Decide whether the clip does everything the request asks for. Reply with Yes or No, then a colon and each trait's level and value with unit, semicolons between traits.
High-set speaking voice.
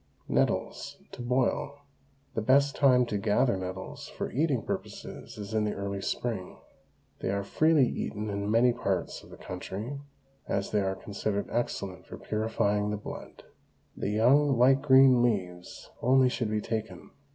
No: low, 110 Hz